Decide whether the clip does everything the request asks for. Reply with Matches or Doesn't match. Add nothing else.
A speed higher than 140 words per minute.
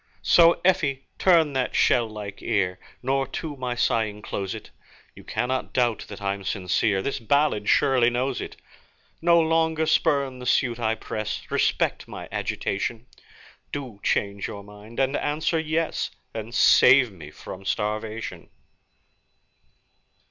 Doesn't match